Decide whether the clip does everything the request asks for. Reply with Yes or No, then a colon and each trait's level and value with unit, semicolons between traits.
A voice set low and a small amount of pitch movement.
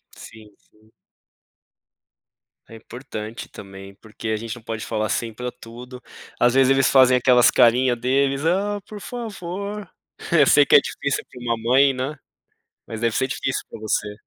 No: low, 125 Hz; average, 3.5 semitones